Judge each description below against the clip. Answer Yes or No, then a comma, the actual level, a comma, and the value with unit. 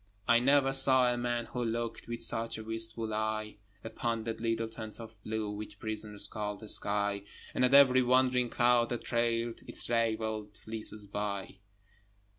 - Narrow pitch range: Yes, narrow, 1.8 semitones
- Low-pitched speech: Yes, low, 115 Hz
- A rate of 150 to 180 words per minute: Yes, average, 165 wpm